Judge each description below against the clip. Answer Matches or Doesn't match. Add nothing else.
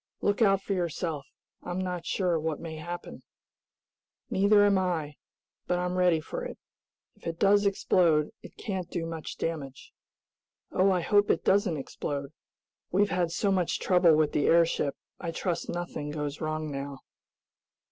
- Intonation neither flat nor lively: Matches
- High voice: Doesn't match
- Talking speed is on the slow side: Doesn't match